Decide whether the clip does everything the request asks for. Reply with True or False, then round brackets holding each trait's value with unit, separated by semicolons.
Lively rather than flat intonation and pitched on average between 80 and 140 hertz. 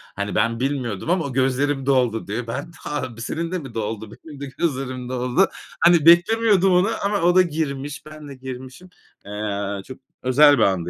True (5.8 semitones; 135 Hz)